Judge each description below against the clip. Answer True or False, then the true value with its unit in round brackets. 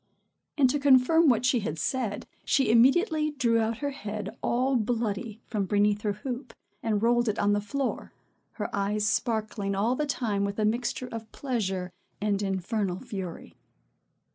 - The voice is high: True (220 Hz)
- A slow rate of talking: False (165 wpm)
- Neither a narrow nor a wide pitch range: True (3.7 semitones)